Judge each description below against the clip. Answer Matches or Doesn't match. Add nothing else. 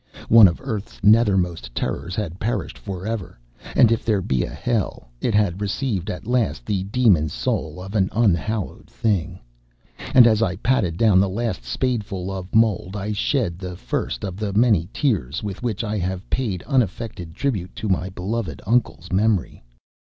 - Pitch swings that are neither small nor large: Matches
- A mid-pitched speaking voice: Doesn't match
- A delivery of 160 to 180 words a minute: Matches